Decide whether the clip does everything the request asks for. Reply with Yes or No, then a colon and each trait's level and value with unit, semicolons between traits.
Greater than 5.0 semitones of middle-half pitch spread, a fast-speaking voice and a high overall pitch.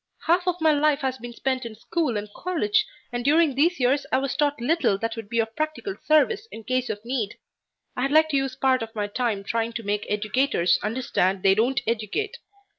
Yes: wide, 5.4 semitones; fast, 210 wpm; very high, 255 Hz